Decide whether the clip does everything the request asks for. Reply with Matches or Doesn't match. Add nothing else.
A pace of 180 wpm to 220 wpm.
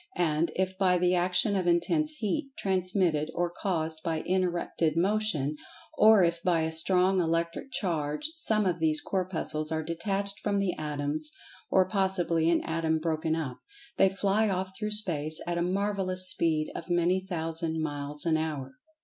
Doesn't match